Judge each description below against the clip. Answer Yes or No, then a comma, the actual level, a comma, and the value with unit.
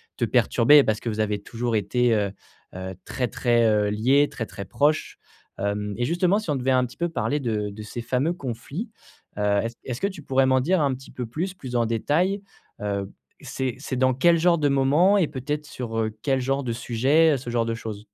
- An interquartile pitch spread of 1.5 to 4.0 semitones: No, average, 4.6 semitones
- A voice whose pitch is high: No, low, 130 Hz